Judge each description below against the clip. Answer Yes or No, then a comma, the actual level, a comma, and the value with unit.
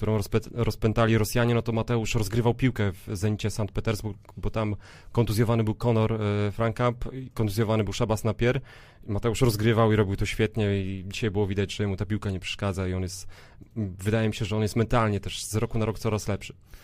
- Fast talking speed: Yes, fast, 200 wpm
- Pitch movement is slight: Yes, narrow, 2.1 semitones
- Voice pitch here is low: Yes, low, 110 Hz